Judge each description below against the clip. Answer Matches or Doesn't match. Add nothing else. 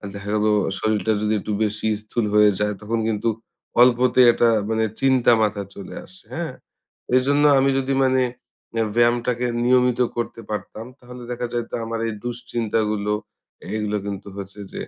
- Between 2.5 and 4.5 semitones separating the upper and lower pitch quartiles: Matches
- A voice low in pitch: Matches